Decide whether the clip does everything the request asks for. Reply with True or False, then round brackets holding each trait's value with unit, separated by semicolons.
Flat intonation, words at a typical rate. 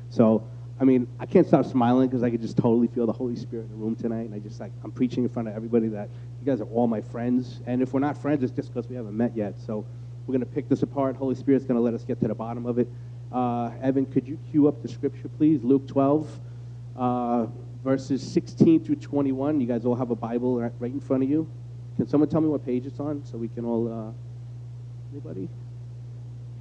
False (1.9 semitones; 245 wpm)